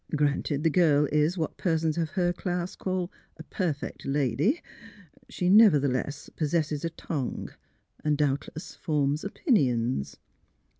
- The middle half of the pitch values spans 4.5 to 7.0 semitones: No, average, 3.5 semitones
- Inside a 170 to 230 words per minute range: No, average, 140 wpm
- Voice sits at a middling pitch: Yes, medium, 155 Hz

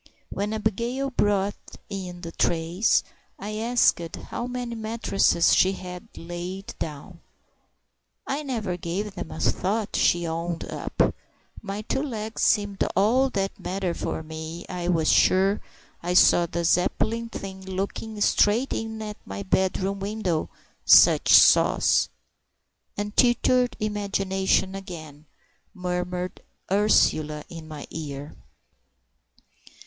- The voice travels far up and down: No, average, 3.7 semitones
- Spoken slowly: Yes, slow, 110 wpm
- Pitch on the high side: Yes, high, 195 Hz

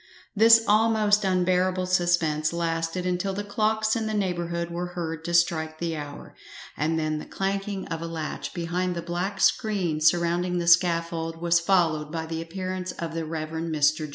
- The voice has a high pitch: No, medium, 170 Hz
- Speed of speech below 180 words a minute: Yes, average, 170 wpm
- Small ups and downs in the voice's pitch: Yes, narrow, 2.3 semitones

